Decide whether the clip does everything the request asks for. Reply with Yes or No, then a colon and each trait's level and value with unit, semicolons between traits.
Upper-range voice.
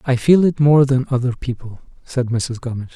No: low, 130 Hz